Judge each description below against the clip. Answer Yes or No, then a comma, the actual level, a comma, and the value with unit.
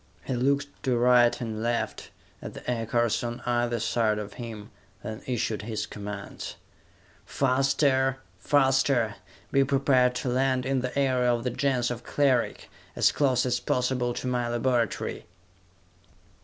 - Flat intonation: Yes, narrow, 2.0 semitones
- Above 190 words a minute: No, average, 140 wpm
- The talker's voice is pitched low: Yes, low, 125 Hz